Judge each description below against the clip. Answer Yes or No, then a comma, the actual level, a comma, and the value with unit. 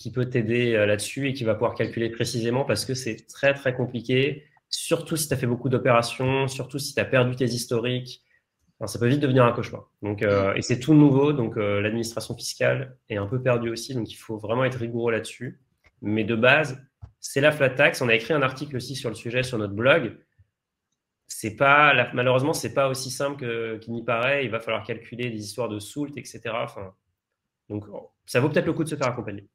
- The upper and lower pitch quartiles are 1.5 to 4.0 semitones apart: Yes, average, 3.0 semitones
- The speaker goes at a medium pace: No, fast, 225 wpm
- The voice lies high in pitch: No, low, 125 Hz